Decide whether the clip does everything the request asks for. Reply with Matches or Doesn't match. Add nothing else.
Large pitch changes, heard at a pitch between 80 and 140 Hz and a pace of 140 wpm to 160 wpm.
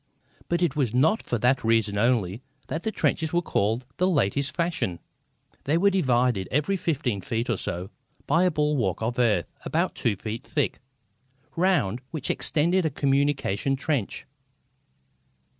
Matches